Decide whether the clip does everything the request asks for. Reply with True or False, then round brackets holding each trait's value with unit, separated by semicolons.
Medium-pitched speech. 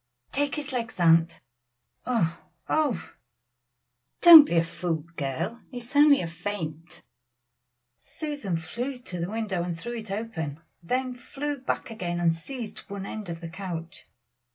False (200 Hz)